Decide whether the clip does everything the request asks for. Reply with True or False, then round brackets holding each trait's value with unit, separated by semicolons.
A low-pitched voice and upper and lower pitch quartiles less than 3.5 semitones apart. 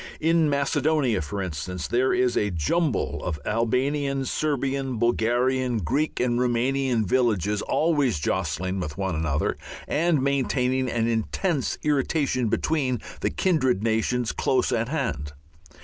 False (125 Hz; 4.8 semitones)